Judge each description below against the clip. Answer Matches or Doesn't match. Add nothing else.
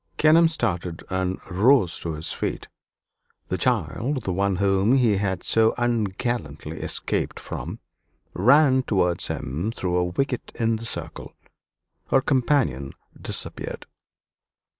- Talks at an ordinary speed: Doesn't match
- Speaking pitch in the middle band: Doesn't match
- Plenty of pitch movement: Matches